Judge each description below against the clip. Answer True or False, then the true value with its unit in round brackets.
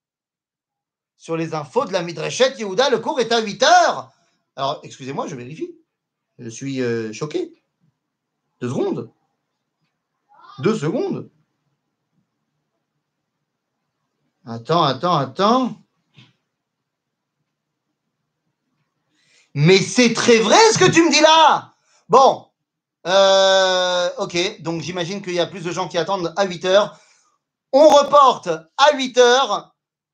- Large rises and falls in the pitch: True (7.2 semitones)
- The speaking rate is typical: False (115 wpm)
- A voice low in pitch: False (190 Hz)